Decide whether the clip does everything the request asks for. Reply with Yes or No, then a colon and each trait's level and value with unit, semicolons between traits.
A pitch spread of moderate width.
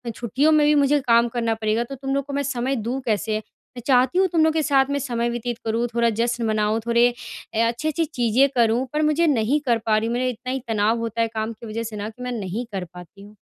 Yes: average, 3.4 semitones